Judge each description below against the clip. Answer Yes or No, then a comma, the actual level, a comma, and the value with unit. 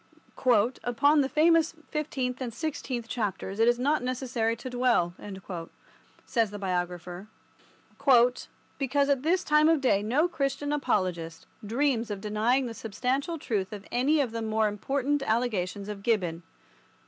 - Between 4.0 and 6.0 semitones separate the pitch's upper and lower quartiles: Yes, average, 5.2 semitones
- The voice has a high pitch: Yes, high, 240 Hz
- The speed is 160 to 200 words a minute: No, average, 140 wpm